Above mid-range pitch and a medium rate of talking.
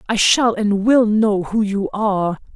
Yes: high, 210 Hz; average, 190 wpm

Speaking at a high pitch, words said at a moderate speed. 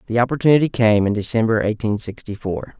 No: low, 115 Hz; average, 170 wpm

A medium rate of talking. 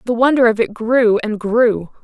Yes: average, 175 wpm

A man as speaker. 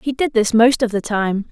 No: female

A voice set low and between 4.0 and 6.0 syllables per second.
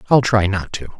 Yes: low, 105 Hz; 5.3 syllables/s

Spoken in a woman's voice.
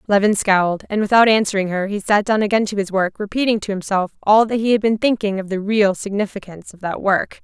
Yes: female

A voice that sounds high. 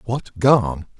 No: low, 110 Hz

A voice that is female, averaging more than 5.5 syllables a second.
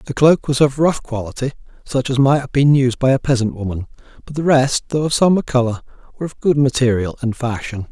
No: male; 6.0 syllables/s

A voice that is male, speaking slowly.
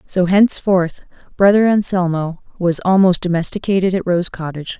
No: female; slow, 125 wpm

